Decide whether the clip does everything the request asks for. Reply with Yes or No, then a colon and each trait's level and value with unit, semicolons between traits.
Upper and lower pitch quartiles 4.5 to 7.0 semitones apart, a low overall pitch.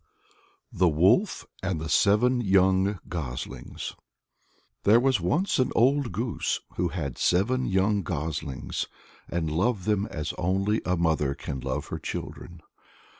Yes: average, 4.9 semitones; very low, 95 Hz